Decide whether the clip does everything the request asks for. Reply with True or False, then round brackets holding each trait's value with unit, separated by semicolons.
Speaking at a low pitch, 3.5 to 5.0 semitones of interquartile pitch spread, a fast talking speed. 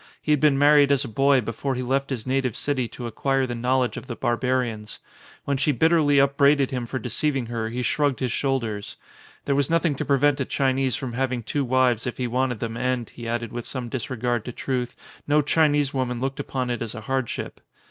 False (130 Hz; 2.5 semitones; 225 wpm)